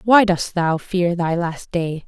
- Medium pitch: Yes, medium, 175 Hz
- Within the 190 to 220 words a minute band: Yes, average, 200 wpm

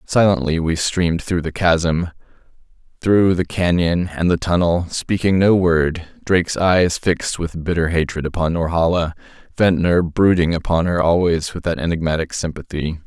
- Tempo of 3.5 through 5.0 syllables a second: Yes, 4.7 syllables/s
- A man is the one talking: Yes, male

